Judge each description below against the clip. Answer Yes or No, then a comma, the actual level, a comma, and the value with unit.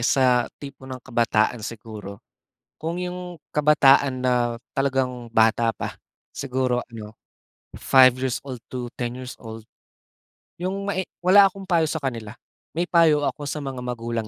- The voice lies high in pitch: No, low, 130 Hz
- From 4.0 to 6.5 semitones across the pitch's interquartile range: Yes, average, 4.4 semitones